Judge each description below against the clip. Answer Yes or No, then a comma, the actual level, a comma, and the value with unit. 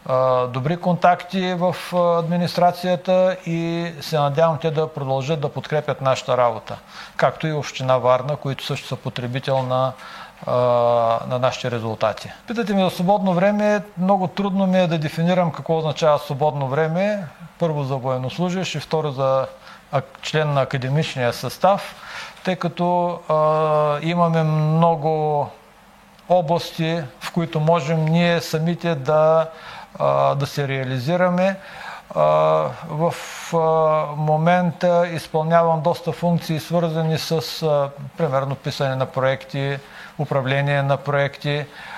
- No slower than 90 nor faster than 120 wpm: Yes, slow, 115 wpm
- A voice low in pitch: No, medium, 155 Hz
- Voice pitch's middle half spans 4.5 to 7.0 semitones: No, average, 4.0 semitones